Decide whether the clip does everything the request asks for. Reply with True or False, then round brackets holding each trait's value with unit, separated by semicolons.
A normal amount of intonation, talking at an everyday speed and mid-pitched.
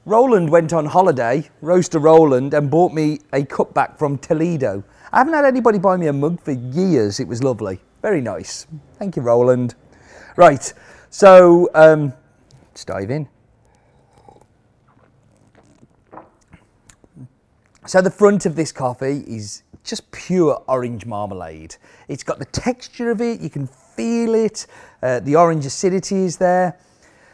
False (6.3 semitones; 145 wpm; 155 Hz)